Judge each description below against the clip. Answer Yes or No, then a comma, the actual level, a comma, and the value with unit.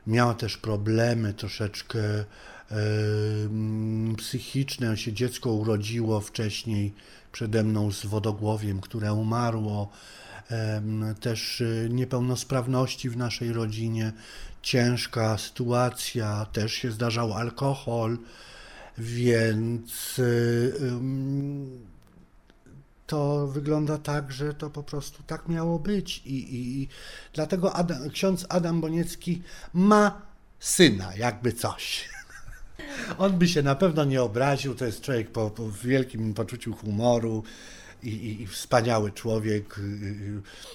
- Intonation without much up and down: No, average, 3.9 semitones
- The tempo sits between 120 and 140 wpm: No, slow, 110 wpm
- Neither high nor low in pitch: No, low, 120 Hz